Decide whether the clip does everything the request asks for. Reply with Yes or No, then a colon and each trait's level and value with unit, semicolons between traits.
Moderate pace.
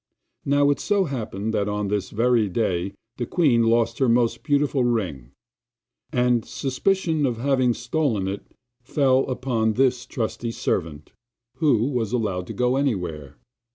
Yes: average, 145 wpm